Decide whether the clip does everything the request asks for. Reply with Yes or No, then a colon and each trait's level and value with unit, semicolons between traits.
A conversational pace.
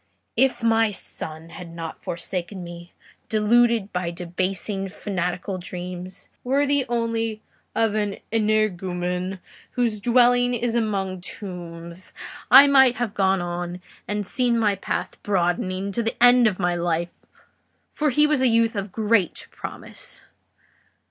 No: slow, 130 wpm